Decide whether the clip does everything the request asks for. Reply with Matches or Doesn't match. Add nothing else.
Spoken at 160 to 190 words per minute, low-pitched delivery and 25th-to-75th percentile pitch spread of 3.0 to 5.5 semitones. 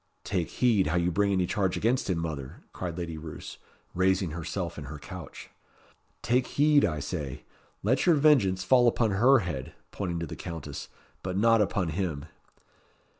Matches